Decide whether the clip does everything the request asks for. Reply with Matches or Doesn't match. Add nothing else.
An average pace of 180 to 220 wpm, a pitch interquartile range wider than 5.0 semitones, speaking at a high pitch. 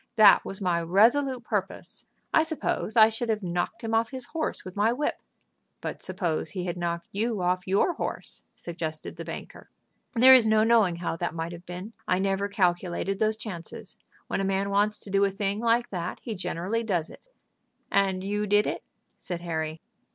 Doesn't match